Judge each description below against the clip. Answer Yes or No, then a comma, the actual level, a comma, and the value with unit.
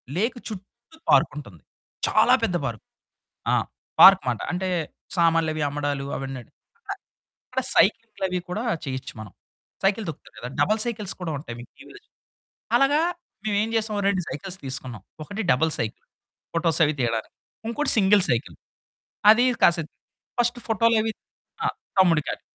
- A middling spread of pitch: No, wide, 7.4 semitones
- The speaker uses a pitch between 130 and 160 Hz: No, medium, 180 Hz